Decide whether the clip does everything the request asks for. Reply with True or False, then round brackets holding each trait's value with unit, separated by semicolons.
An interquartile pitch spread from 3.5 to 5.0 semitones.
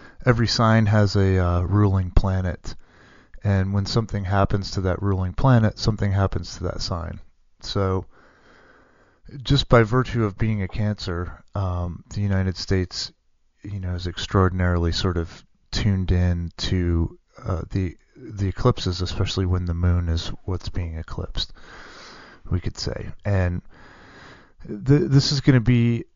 False (2.9 semitones)